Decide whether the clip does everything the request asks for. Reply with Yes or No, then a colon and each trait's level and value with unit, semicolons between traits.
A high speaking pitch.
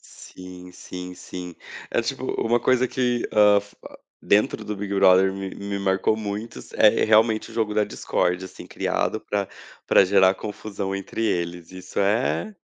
No: low, 100 Hz